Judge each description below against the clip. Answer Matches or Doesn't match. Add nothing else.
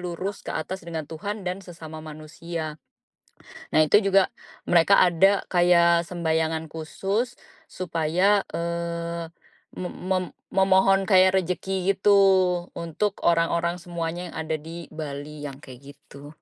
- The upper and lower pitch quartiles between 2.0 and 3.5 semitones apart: Matches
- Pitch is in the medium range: Matches